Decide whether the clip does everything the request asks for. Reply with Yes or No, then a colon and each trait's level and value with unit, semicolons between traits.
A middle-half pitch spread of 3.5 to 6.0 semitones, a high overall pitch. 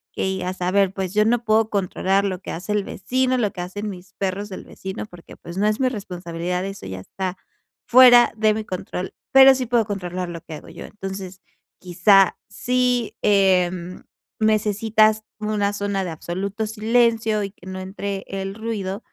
No: average, 2.7 semitones; high, 200 Hz